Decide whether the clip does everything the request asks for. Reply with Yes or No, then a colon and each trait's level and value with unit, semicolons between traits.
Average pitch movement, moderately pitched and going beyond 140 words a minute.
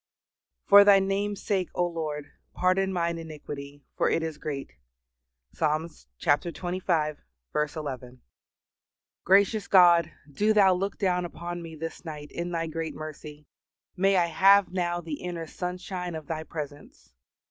No: average, 3.3 semitones; medium, 170 Hz; slow, 135 wpm